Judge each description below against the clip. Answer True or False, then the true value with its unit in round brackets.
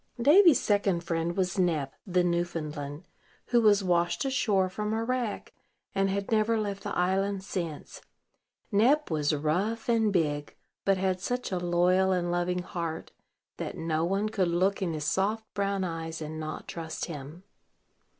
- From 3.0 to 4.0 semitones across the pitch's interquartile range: True (3.5 semitones)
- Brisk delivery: False (160 wpm)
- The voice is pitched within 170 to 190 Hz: True (185 Hz)